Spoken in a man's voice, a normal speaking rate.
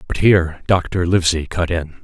Yes: male; average, 175 wpm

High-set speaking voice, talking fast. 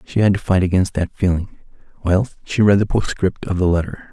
No: very low, 95 Hz; fast, 220 wpm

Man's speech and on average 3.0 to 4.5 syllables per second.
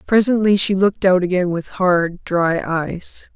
No: female; 4.1 syllables/s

